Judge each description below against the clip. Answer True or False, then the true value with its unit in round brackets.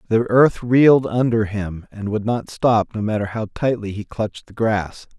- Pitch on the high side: False (110 Hz)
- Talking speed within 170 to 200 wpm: True (195 wpm)